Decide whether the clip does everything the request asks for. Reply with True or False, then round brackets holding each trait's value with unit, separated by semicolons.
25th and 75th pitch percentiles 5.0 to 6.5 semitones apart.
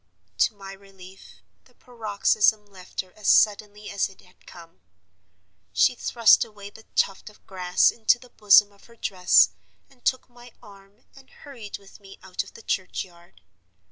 False (2.5 semitones)